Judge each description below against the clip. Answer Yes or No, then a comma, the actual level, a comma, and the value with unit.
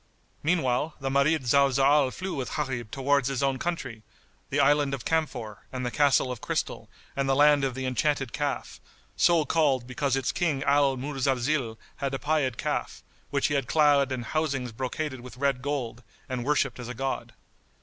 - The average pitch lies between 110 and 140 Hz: Yes, low, 135 Hz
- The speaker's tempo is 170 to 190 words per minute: Yes, average, 180 wpm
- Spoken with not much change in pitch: Yes, narrow, 2.3 semitones